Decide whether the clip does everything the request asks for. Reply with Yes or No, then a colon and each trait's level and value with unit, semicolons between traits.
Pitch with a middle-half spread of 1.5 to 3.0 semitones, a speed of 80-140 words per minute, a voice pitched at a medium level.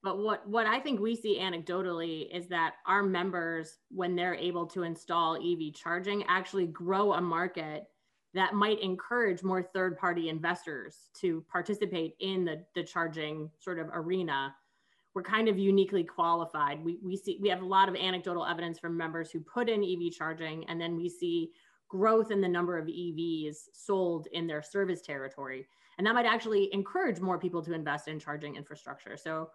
No: average, 2.7 semitones; average, 180 wpm; medium, 175 Hz